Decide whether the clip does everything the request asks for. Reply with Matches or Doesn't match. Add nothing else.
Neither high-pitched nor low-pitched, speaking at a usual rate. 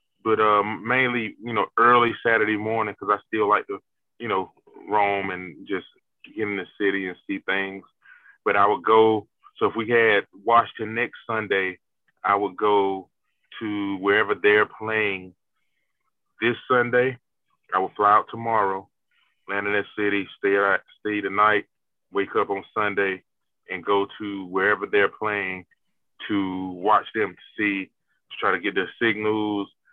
Doesn't match